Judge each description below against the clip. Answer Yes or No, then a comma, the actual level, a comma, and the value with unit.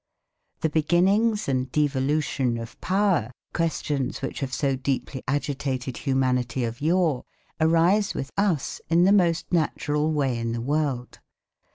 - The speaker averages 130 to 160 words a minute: Yes, slow, 135 wpm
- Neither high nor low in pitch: Yes, medium, 145 Hz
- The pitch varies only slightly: No, average, 4.3 semitones